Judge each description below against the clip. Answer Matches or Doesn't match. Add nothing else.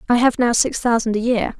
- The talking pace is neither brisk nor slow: Doesn't match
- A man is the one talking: Doesn't match